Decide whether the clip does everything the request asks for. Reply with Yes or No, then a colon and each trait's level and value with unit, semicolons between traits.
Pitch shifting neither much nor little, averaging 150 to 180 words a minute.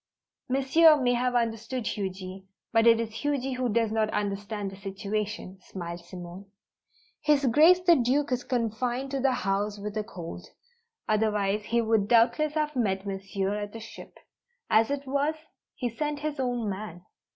Yes: average, 4.6 semitones; average, 160 wpm